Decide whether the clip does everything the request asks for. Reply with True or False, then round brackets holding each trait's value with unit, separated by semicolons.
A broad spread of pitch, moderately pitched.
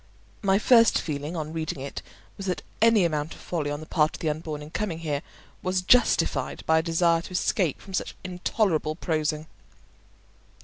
False (3.2 semitones; 165 Hz)